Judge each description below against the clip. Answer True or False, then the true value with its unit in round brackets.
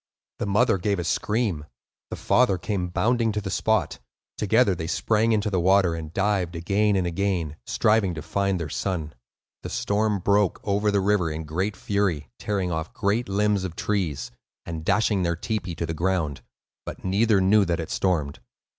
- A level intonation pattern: False (3.4 semitones)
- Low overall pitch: True (95 Hz)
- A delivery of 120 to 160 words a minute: False (180 wpm)